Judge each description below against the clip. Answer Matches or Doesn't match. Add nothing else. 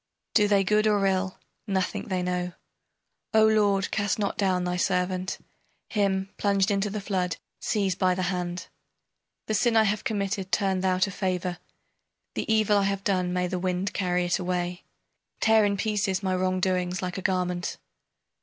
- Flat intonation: Matches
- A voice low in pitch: Doesn't match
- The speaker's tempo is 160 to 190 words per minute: Matches